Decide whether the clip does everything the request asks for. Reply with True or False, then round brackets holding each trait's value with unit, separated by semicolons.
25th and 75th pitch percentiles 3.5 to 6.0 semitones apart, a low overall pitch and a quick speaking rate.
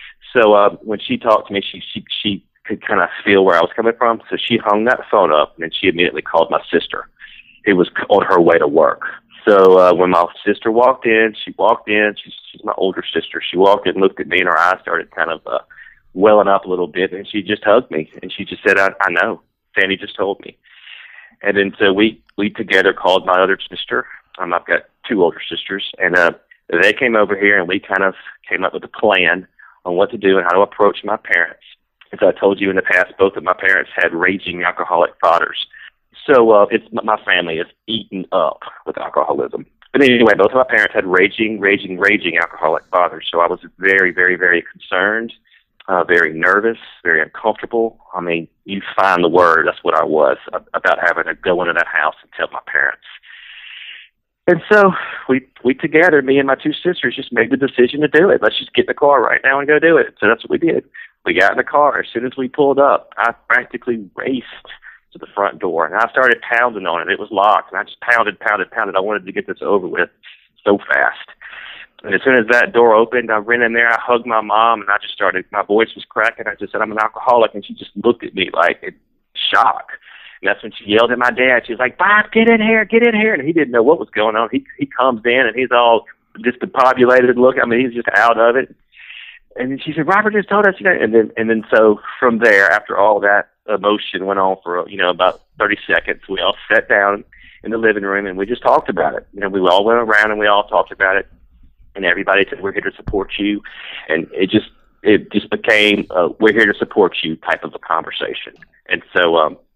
True (4.3 semitones; 110 Hz; 240 wpm)